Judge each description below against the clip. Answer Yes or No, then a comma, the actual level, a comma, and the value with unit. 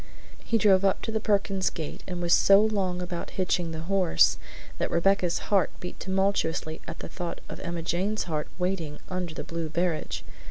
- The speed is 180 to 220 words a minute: Yes, average, 185 wpm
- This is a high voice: No, medium, 180 Hz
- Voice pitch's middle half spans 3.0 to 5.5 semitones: No, narrow, 2.6 semitones